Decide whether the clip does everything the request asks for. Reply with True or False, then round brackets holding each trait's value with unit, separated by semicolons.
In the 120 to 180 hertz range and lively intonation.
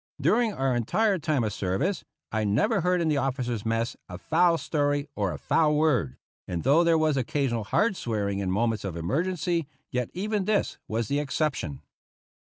True (140 Hz; 7.1 semitones)